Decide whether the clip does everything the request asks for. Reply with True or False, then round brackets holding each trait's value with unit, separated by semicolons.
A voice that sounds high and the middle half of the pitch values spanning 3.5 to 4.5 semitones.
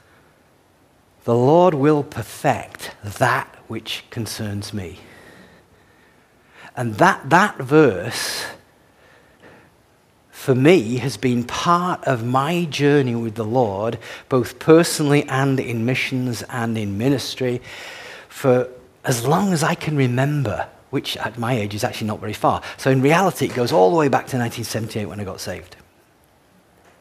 False (125 Hz; 4.1 semitones)